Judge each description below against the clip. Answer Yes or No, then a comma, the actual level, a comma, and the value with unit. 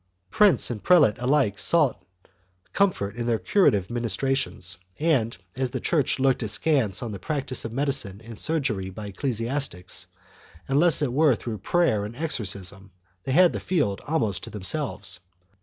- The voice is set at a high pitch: No, low, 120 Hz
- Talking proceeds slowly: No, average, 155 wpm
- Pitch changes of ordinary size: No, wide, 6.1 semitones